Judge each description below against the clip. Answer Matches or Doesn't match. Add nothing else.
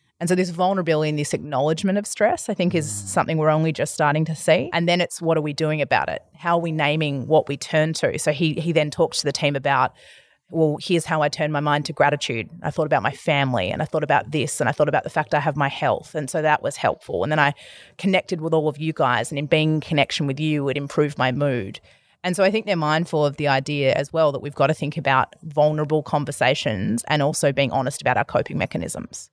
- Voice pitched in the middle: Matches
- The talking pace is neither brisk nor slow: Doesn't match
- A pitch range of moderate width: Doesn't match